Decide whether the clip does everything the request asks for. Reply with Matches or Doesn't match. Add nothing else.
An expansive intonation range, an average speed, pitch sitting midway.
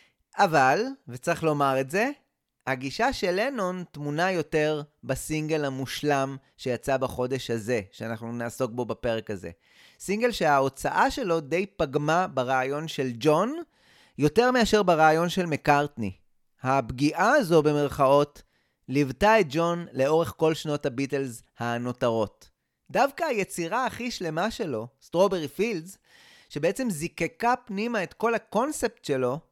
Matches